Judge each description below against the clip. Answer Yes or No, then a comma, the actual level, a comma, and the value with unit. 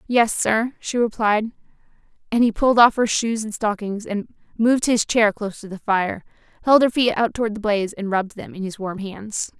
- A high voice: Yes, high, 215 Hz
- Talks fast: Yes, fast, 215 wpm